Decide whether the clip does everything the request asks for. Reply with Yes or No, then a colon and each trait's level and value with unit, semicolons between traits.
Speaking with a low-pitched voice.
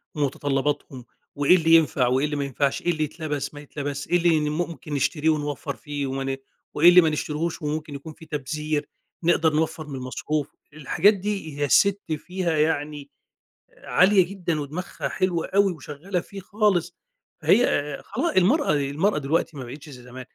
No: medium, 155 Hz